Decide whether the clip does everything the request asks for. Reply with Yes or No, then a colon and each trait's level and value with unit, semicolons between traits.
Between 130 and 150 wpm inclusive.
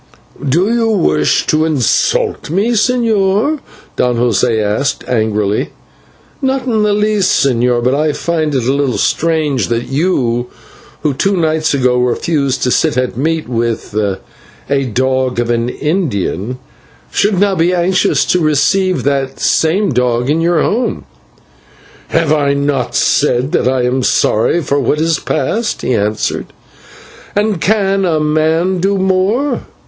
Yes: average, 145 wpm